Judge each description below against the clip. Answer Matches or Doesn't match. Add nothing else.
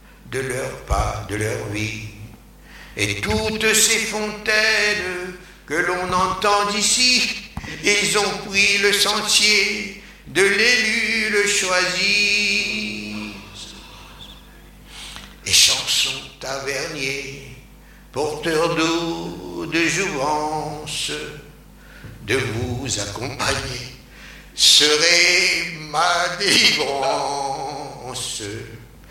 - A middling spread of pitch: Doesn't match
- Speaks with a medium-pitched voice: Matches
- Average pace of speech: Doesn't match